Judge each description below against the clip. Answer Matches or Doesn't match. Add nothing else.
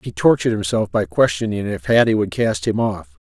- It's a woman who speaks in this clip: Doesn't match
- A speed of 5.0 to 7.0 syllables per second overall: Matches